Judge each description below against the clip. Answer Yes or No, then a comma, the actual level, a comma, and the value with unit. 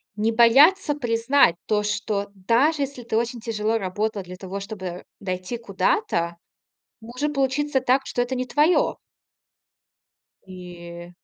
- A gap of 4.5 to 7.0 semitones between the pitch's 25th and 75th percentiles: Yes, average, 5.3 semitones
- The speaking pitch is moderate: No, high, 225 Hz